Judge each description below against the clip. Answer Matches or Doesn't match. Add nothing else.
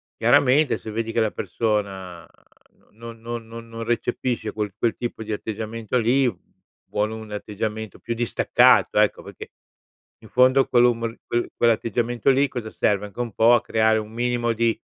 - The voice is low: Matches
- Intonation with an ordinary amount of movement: Doesn't match